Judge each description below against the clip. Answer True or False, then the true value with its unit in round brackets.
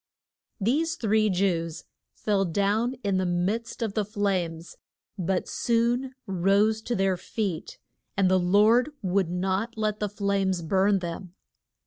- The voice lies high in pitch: True (200 Hz)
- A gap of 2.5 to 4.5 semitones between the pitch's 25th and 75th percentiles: True (2.9 semitones)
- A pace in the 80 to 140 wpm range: True (135 wpm)